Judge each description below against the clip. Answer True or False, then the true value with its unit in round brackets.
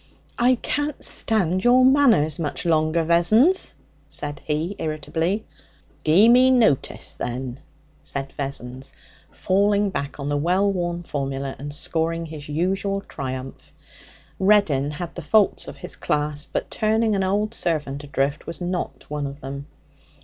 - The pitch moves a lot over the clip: True (5.8 semitones)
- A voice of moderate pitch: True (165 Hz)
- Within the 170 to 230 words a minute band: False (140 wpm)